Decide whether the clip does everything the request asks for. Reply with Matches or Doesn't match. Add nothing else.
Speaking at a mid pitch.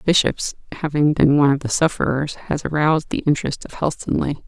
Matches